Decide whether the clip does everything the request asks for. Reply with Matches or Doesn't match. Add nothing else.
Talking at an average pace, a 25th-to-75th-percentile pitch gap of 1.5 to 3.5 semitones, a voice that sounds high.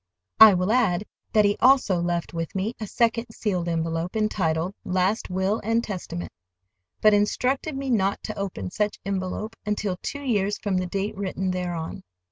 Matches